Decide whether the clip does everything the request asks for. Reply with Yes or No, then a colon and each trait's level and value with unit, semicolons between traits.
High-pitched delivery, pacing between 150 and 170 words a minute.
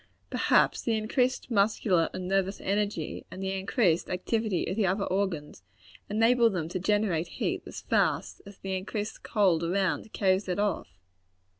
Yes: high, 195 Hz; average, 155 wpm